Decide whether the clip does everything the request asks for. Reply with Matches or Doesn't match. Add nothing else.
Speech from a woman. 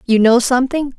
Matches